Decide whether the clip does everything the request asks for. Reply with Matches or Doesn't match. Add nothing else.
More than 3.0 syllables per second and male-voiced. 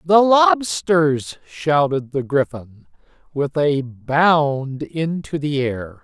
Doesn't match